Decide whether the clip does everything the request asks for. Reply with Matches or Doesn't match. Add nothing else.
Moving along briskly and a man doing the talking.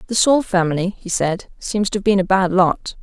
Doesn't match